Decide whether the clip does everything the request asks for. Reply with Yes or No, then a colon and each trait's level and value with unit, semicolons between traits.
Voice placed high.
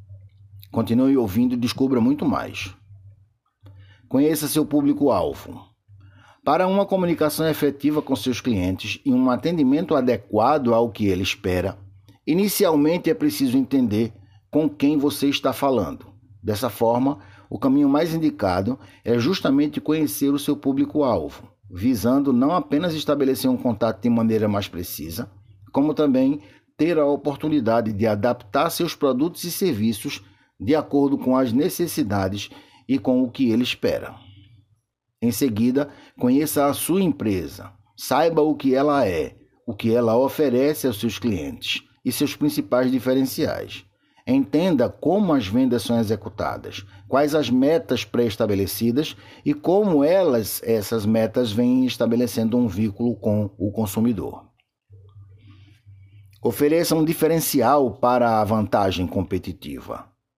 No: low, 125 Hz